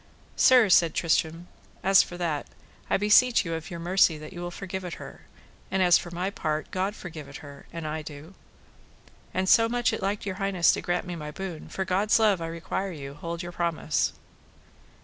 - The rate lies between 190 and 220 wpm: Yes, fast, 205 wpm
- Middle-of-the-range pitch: Yes, medium, 175 Hz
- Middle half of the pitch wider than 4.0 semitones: No, average, 2.9 semitones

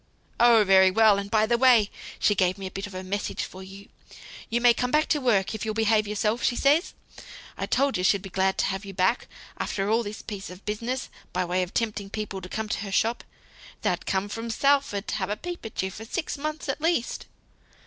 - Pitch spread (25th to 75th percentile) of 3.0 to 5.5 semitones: Yes, average, 3.6 semitones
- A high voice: Yes, high, 210 Hz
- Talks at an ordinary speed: No, fast, 235 wpm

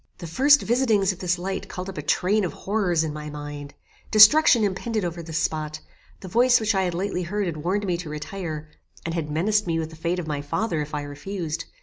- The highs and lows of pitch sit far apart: No, average, 4.6 semitones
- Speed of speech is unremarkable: No, fast, 230 wpm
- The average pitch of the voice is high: No, medium, 175 Hz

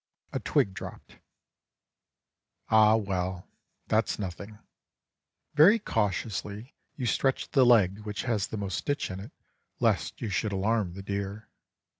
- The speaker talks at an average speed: No, slow, 130 wpm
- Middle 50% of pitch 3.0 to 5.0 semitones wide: No, narrow, 2.6 semitones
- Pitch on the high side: No, low, 105 Hz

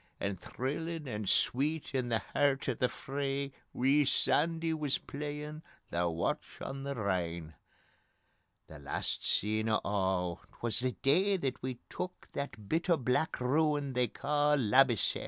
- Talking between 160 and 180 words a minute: No, average, 150 wpm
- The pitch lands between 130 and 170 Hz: Yes, low, 135 Hz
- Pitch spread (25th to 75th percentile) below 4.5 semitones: No, wide, 5.6 semitones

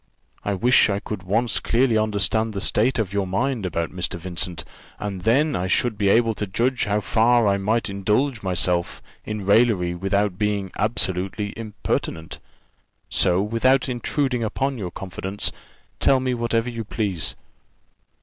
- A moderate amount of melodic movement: Yes, average, 3.5 semitones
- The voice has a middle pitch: No, low, 105 Hz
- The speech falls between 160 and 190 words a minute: No, average, 150 wpm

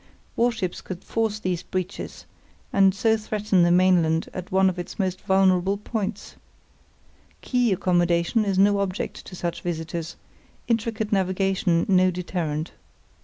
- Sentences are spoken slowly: Yes, slow, 130 wpm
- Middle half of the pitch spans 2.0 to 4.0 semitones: Yes, narrow, 2.5 semitones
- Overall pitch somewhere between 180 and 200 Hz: Yes, medium, 185 Hz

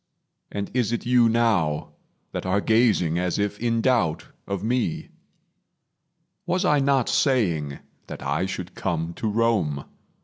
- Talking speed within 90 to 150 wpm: Yes, average, 140 wpm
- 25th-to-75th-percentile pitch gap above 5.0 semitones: Yes, wide, 5.5 semitones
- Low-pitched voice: Yes, low, 105 Hz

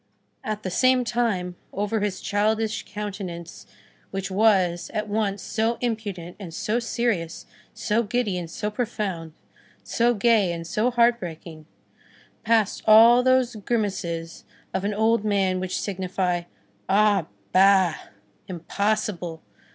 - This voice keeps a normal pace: No, slow, 125 wpm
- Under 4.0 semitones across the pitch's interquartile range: Yes, average, 3.6 semitones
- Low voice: No, high, 205 Hz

